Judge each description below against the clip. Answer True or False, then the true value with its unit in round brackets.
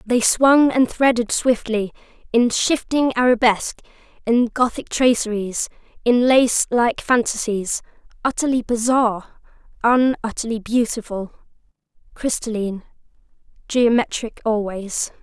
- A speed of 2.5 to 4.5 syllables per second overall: True (4.4 syllables/s)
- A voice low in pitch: False (235 Hz)